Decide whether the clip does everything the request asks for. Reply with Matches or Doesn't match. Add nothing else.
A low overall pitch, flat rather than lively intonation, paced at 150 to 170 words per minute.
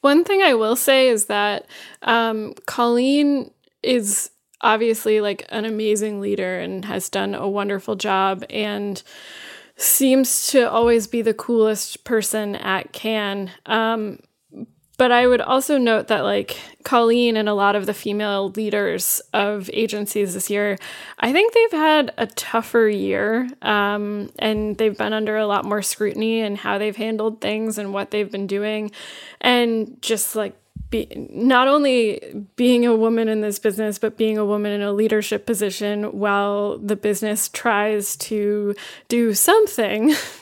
Doesn't match